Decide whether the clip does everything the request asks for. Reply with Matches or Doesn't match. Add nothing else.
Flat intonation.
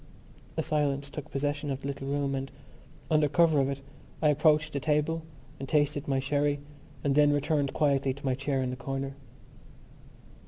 Matches